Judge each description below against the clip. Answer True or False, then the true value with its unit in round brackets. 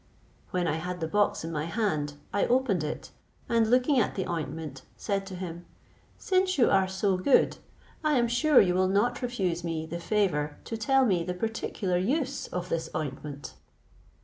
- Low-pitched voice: False (190 Hz)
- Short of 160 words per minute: False (180 wpm)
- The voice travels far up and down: True (5.9 semitones)